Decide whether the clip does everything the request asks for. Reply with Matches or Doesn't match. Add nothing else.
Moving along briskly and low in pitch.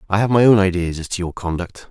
Matches